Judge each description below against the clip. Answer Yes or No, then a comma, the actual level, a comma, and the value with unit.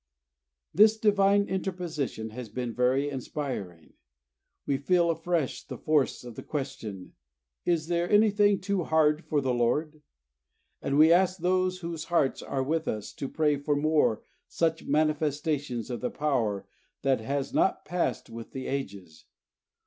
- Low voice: No, medium, 150 Hz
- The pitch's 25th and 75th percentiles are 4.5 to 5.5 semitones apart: Yes, average, 5.0 semitones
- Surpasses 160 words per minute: No, average, 140 wpm